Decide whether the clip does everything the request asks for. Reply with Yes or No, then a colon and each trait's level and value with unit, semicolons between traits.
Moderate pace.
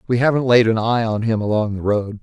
No: fast, 270 wpm